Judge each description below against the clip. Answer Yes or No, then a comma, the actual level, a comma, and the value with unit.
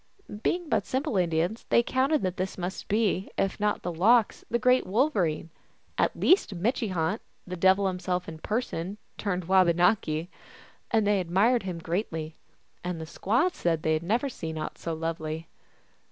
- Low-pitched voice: No, medium, 185 Hz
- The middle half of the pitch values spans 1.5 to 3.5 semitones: No, average, 5.0 semitones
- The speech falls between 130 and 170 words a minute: Yes, average, 160 wpm